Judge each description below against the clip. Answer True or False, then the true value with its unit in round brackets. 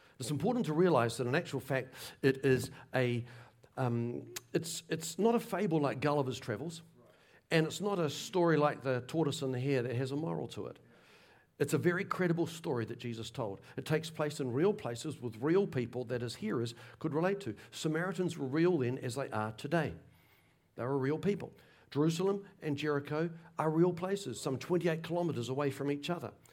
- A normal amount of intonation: True (4.7 semitones)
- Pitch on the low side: False (145 Hz)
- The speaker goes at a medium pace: True (190 wpm)